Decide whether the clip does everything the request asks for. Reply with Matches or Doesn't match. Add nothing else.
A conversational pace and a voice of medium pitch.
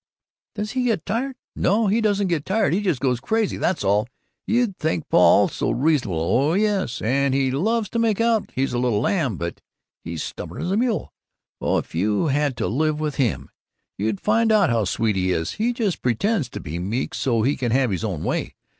Doesn't match